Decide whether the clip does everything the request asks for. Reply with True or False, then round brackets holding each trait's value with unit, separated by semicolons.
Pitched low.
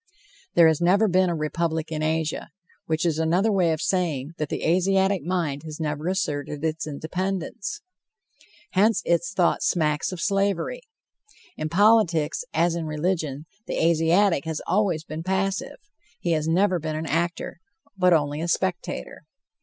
False (170 Hz)